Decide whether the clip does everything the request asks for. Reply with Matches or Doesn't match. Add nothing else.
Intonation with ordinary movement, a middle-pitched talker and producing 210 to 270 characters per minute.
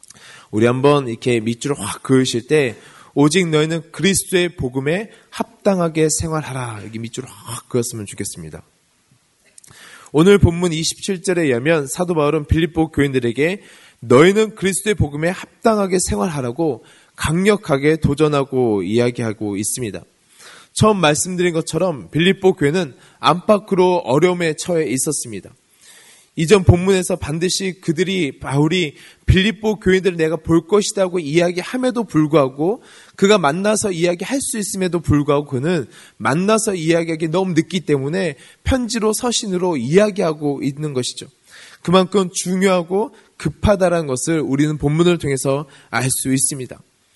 Doesn't match